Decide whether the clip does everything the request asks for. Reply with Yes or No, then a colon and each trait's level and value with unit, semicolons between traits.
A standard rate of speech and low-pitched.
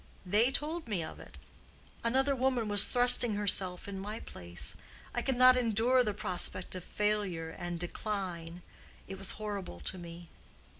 No: average, 155 wpm; high, 205 Hz